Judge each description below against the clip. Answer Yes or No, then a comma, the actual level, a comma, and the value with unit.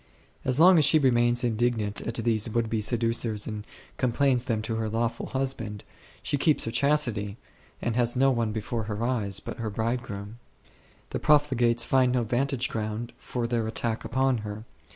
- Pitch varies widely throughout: No, narrow, 2.5 semitones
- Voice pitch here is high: No, low, 115 Hz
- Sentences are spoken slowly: No, average, 180 wpm